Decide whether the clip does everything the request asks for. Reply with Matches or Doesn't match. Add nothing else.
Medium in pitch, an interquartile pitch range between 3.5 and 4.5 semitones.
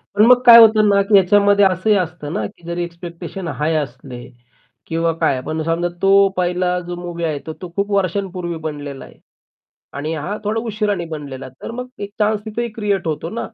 Matches